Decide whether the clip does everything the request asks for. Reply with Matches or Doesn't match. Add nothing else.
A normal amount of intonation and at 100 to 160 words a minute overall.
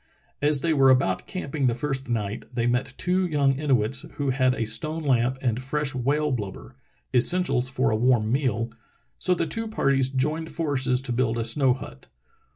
Doesn't match